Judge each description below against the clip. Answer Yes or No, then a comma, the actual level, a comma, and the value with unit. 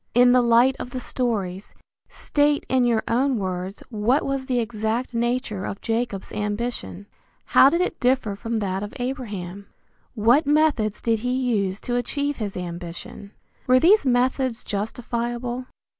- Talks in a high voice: Yes, high, 235 Hz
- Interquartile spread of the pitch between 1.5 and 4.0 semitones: Yes, average, 3.6 semitones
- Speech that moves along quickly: No, average, 150 wpm